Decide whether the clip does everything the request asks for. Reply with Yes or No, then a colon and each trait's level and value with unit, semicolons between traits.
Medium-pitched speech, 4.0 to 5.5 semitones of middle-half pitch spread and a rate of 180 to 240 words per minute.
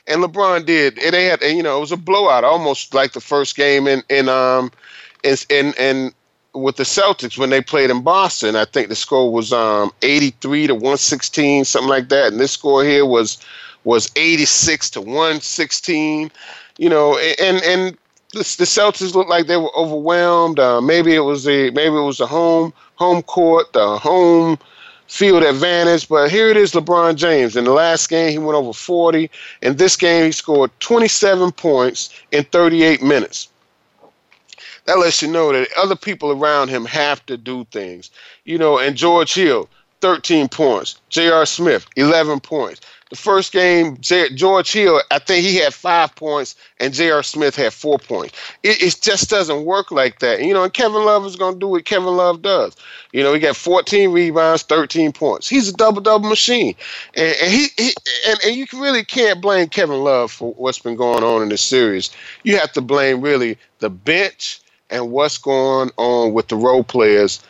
Yes: medium, 160 Hz; average, 5.2 semitones; average, 190 wpm